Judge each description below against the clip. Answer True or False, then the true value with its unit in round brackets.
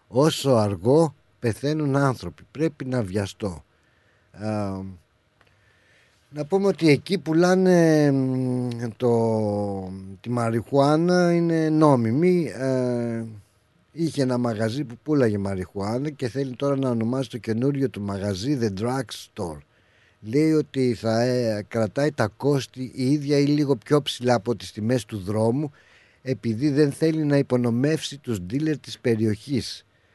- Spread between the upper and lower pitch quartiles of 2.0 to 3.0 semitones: False (4.9 semitones)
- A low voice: True (125 Hz)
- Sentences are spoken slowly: False (125 wpm)